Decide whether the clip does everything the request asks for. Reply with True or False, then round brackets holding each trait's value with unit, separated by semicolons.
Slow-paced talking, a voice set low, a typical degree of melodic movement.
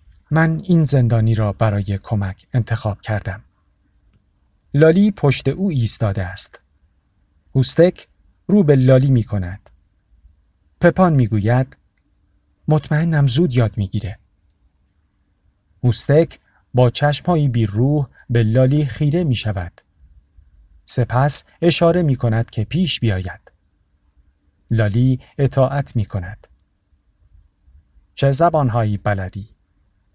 False (100 wpm; 105 Hz; 7.3 semitones)